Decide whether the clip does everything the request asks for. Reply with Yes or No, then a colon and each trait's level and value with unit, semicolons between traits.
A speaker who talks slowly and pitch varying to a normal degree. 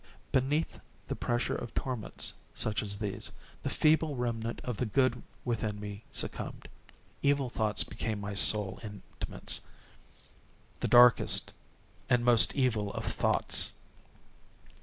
Yes: slow, 120 wpm; average, 3.4 semitones